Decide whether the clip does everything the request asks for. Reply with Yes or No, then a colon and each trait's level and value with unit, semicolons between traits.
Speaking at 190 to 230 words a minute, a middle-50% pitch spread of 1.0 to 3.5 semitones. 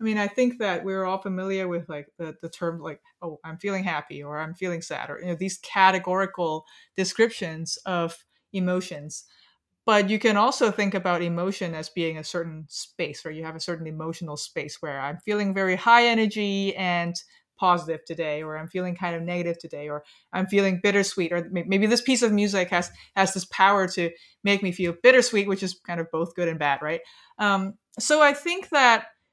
Yes: average, 200 wpm; average, 3.2 semitones